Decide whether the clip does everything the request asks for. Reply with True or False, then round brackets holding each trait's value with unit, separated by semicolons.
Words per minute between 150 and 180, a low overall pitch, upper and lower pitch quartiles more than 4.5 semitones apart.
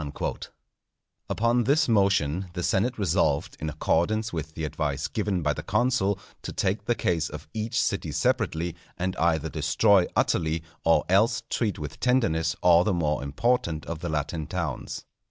True (160 wpm; 85 Hz; 5.3 semitones)